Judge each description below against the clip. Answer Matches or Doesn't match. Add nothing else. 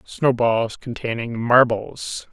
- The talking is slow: Matches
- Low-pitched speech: Matches